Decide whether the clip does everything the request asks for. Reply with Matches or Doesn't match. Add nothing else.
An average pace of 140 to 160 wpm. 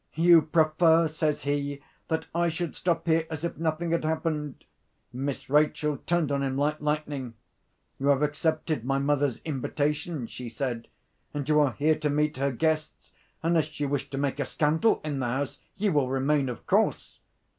Doesn't match